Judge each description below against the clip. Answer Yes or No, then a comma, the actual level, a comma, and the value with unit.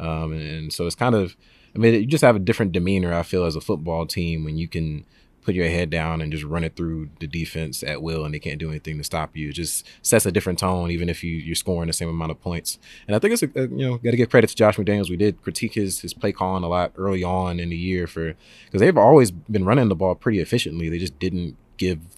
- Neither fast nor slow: No, fast, 280 wpm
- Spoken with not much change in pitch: No, average, 3.8 semitones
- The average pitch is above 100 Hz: No, very low, 85 Hz